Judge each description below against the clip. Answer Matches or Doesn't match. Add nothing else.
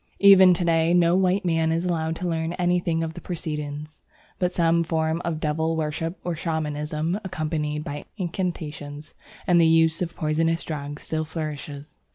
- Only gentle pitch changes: Matches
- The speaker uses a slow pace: Doesn't match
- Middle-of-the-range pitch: Matches